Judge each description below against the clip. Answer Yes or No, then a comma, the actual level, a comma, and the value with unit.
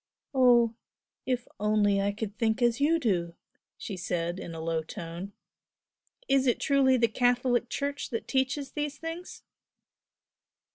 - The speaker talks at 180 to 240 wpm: No, average, 140 wpm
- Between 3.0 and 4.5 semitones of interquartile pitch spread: No, average, 5.2 semitones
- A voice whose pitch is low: No, high, 240 Hz